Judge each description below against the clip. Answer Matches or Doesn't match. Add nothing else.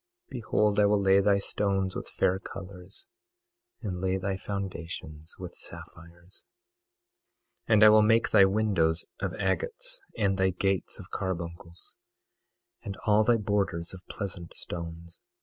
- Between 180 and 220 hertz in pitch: Doesn't match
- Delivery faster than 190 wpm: Doesn't match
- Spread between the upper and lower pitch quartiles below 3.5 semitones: Matches